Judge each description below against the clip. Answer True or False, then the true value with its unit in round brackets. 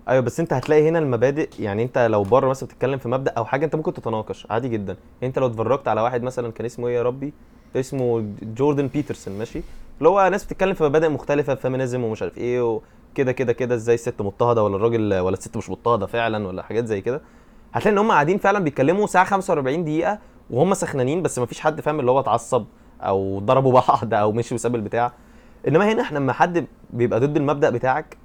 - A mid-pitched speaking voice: False (125 Hz)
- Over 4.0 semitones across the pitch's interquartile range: True (4.5 semitones)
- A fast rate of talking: True (210 wpm)